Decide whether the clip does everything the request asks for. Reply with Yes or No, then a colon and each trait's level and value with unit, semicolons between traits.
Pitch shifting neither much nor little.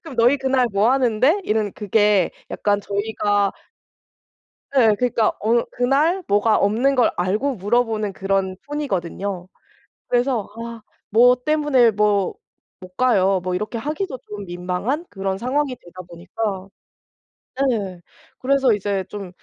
Yes: average, 4.4 semitones